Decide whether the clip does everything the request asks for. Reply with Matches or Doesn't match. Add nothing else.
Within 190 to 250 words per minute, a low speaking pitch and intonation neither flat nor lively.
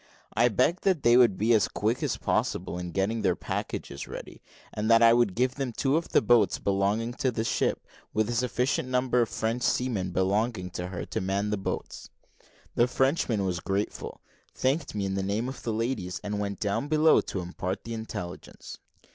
Matches